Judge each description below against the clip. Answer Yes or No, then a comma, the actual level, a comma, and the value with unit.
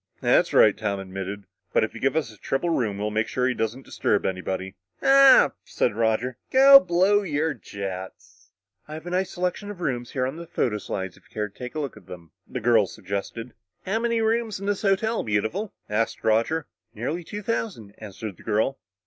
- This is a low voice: Yes, low, 125 Hz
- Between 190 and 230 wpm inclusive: Yes, average, 195 wpm